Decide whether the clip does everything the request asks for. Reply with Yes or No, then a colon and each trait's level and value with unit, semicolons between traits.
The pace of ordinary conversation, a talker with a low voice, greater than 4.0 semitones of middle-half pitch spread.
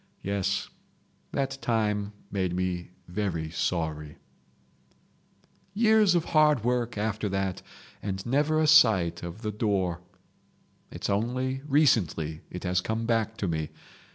No: slow, 125 wpm; low, 105 Hz; wide, 5.6 semitones